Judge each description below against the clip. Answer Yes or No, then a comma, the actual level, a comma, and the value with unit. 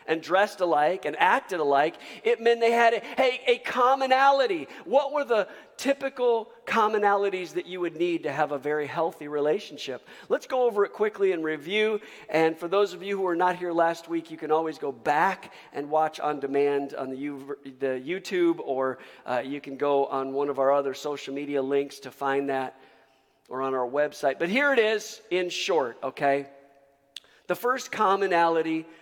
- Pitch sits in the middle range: Yes, medium, 165 Hz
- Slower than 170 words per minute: No, average, 190 wpm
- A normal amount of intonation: No, wide, 7.0 semitones